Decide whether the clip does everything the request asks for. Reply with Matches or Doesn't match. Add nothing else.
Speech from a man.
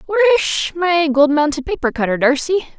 Doesn't match